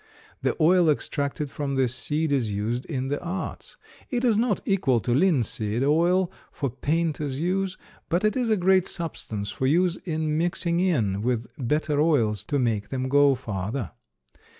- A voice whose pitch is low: No, medium, 145 Hz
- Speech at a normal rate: Yes, average, 165 wpm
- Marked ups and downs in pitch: Yes, wide, 5.7 semitones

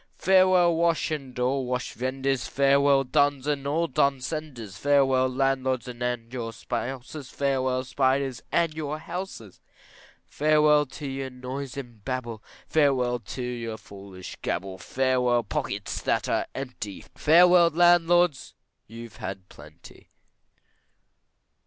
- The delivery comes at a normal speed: No, slow, 120 wpm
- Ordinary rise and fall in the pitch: Yes, average, 3.2 semitones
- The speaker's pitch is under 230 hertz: Yes, low, 135 Hz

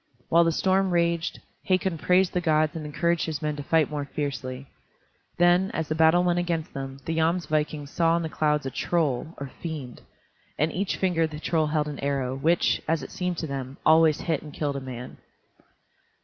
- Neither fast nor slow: Yes, average, 195 wpm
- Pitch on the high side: No, medium, 160 Hz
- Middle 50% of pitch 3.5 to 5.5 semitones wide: No, average, 2.8 semitones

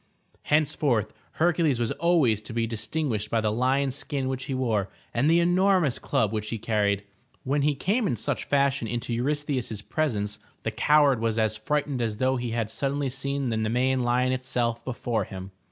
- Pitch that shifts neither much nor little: Yes, average, 4.2 semitones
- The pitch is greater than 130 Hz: No, low, 125 Hz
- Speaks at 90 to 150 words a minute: No, average, 180 wpm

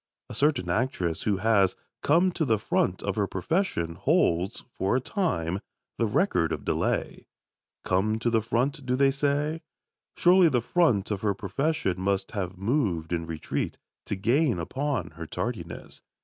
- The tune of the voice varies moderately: No, wide, 7.4 semitones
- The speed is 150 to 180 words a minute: Yes, average, 160 wpm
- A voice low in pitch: Yes, low, 110 Hz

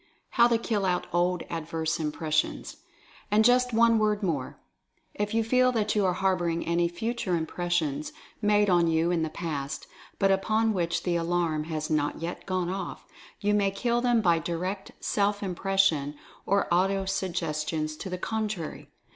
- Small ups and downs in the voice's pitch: No, average, 3.9 semitones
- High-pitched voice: No, medium, 180 Hz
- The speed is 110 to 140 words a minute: No, average, 165 wpm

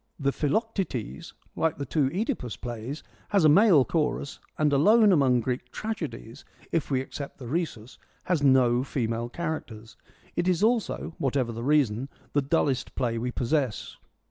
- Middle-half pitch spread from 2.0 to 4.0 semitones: No, average, 5.1 semitones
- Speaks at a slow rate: No, average, 160 wpm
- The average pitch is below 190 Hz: Yes, medium, 140 Hz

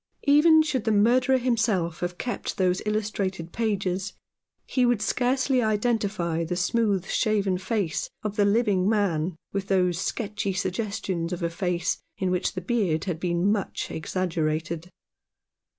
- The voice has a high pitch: Yes, high, 195 Hz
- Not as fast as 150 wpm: Yes, average, 140 wpm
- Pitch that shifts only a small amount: No, average, 3.7 semitones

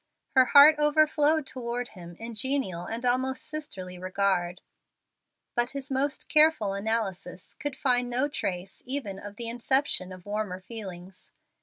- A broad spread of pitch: Yes, wide, 6.2 semitones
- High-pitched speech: Yes, high, 235 Hz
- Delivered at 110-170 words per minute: Yes, average, 145 wpm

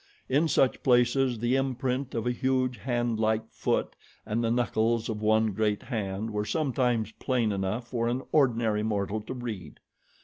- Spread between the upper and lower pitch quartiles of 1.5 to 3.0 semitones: Yes, average, 2.7 semitones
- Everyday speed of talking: Yes, average, 160 wpm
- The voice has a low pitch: Yes, low, 115 Hz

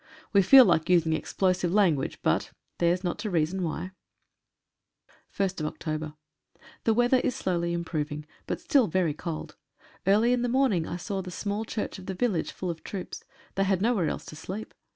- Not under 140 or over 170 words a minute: No, average, 180 wpm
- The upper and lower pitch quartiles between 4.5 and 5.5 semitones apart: No, average, 3.9 semitones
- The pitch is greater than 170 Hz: Yes, medium, 185 Hz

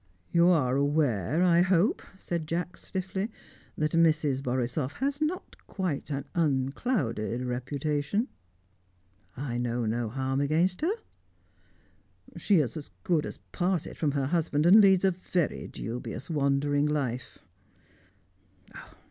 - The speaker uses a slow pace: Yes, slow, 120 wpm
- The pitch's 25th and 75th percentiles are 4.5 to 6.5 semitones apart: Yes, average, 5.1 semitones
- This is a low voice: No, medium, 150 Hz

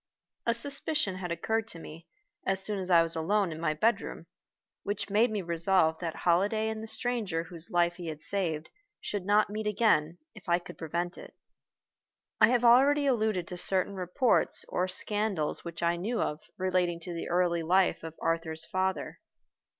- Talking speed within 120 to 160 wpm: No, average, 180 wpm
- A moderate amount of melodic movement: Yes, average, 4.0 semitones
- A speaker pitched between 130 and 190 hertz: Yes, medium, 185 Hz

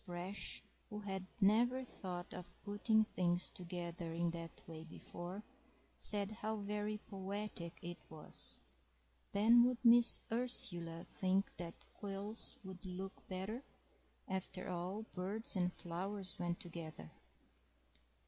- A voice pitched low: No, high, 190 Hz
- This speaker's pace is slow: Yes, slow, 120 wpm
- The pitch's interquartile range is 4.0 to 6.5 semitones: No, average, 3.2 semitones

